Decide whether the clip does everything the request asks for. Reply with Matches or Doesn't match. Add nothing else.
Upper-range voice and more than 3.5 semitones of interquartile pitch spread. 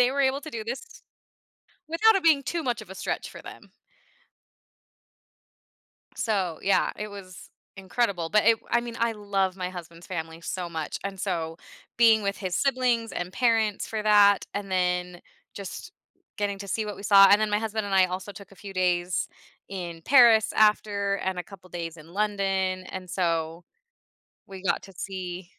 Doesn't match